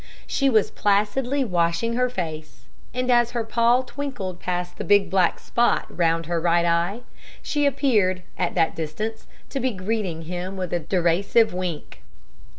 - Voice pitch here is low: No, high, 190 Hz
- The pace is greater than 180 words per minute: No, average, 155 wpm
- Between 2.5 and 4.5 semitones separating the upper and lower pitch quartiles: No, wide, 5.5 semitones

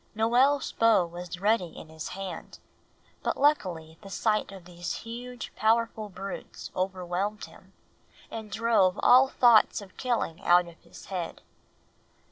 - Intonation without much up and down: No, average, 4.4 semitones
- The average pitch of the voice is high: Yes, high, 200 Hz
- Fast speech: No, slow, 135 wpm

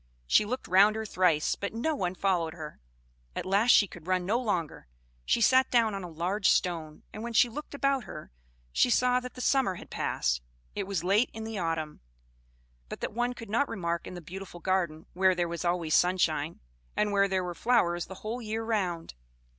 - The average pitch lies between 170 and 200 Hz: Yes, high, 190 Hz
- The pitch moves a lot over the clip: No, average, 4.6 semitones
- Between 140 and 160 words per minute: No, fast, 205 wpm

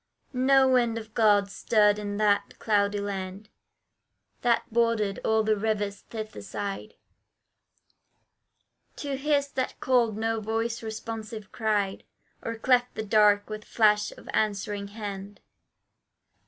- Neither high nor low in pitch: No, high, 215 Hz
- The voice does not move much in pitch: Yes, narrow, 2.0 semitones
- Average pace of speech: No, slow, 120 wpm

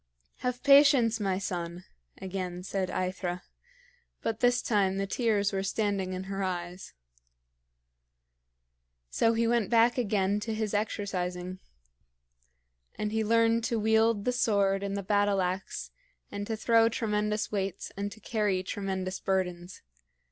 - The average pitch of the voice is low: No, high, 205 Hz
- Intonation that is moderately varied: Yes, average, 3.0 semitones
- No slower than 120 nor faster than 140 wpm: Yes, slow, 135 wpm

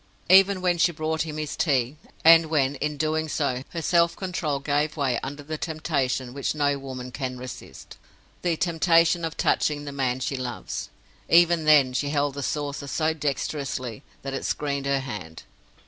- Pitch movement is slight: No, average, 3.0 semitones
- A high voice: No, medium, 145 Hz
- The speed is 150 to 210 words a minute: Yes, average, 165 wpm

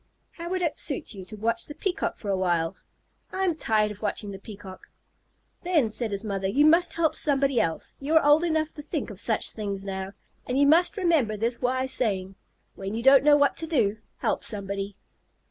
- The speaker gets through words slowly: No, fast, 205 wpm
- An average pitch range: No, wide, 7.4 semitones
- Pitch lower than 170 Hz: No, high, 235 Hz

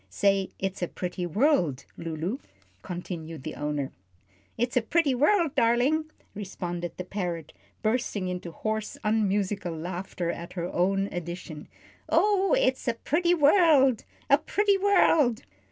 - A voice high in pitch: Yes, high, 200 Hz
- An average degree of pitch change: No, wide, 7.5 semitones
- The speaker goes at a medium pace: No, slow, 130 wpm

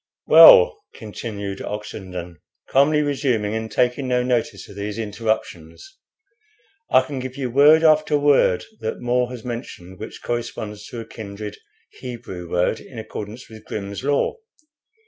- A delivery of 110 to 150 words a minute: Yes, average, 140 wpm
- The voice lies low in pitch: Yes, low, 115 Hz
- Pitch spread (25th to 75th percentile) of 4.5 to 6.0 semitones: No, average, 4.0 semitones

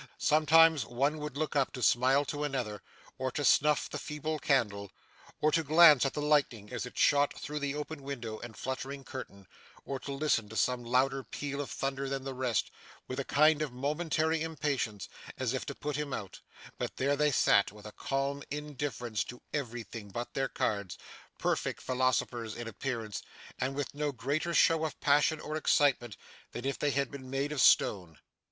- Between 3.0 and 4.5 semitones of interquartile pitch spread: Yes, average, 3.4 semitones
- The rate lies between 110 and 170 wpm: No, average, 185 wpm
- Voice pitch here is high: No, low, 135 Hz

